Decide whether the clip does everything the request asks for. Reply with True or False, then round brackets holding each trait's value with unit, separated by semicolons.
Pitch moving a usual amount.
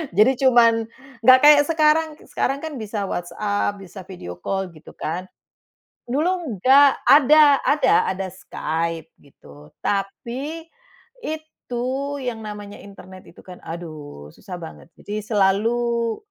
False (6.7 semitones)